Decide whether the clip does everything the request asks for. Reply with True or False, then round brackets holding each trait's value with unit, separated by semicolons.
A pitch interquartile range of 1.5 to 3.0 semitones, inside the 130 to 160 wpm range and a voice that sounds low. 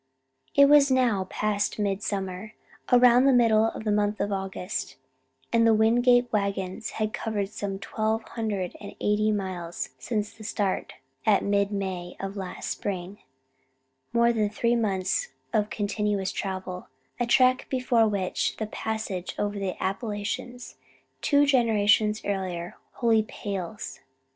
False (2.7 semitones; 140 wpm; 210 Hz)